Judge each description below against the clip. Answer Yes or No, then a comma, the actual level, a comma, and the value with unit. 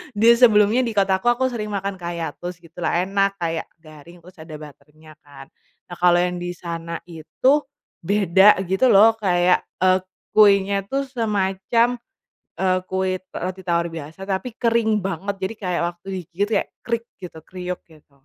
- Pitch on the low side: No, medium, 185 Hz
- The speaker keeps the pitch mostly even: No, average, 3.0 semitones